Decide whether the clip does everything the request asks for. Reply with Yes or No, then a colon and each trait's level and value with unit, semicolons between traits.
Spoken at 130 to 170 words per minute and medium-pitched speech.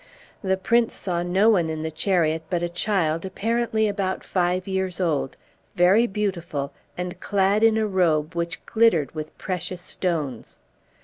Yes: average, 150 wpm; medium, 180 Hz